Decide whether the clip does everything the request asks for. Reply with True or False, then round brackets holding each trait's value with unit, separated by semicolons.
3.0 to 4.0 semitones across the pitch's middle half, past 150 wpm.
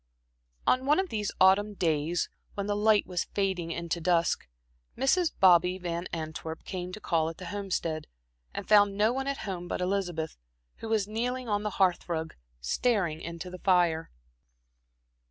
True (3.6 semitones; 165 wpm)